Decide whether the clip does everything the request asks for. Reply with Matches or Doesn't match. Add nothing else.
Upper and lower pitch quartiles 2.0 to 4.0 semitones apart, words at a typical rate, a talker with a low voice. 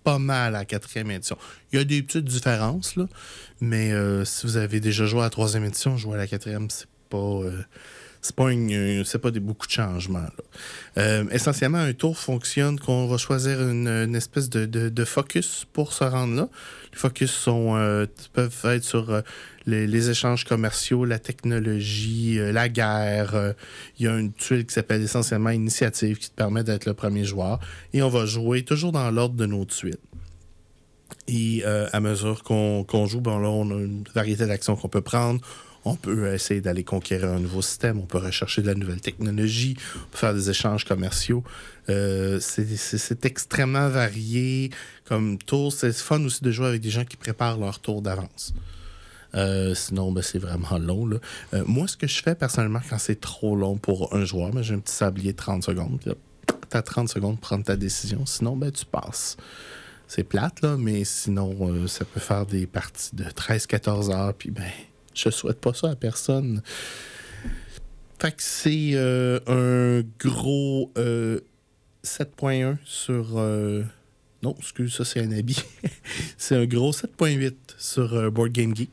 Matches